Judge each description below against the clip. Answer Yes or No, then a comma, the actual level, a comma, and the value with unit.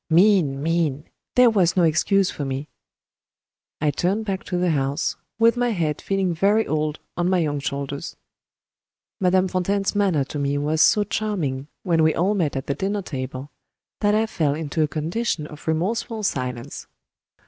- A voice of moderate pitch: Yes, medium, 165 Hz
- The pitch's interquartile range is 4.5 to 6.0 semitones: Yes, average, 5.2 semitones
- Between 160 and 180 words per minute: Yes, average, 170 wpm